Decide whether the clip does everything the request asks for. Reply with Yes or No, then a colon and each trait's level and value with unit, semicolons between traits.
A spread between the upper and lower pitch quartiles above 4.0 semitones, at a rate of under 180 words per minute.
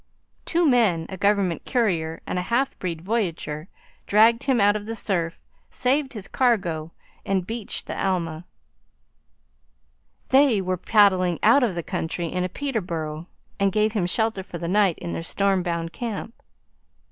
Yes: average, 4.9 semitones; average, 160 wpm